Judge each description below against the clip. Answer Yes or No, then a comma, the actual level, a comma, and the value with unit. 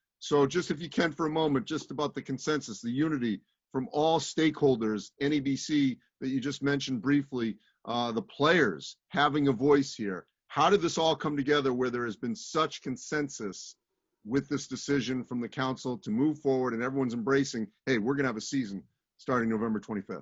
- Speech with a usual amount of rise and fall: Yes, average, 3.2 semitones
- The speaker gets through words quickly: No, average, 190 wpm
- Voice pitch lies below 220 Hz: Yes, low, 135 Hz